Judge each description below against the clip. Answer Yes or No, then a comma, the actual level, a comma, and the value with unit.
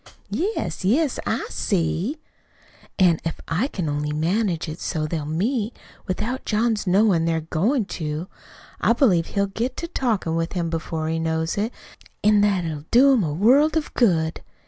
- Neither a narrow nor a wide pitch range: No, wide, 6.0 semitones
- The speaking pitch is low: No, medium, 185 Hz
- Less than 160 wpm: No, average, 170 wpm